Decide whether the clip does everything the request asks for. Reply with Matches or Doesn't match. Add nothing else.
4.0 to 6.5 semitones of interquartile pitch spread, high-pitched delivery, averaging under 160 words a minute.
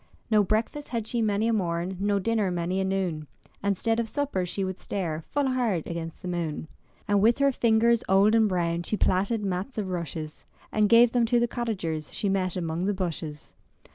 Doesn't match